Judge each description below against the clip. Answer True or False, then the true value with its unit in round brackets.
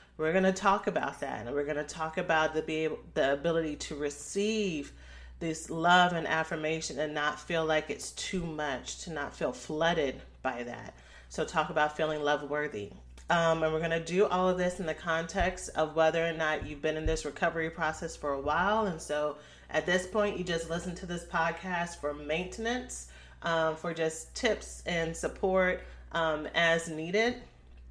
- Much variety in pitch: False (2.8 semitones)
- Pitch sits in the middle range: True (160 Hz)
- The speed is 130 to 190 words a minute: True (185 wpm)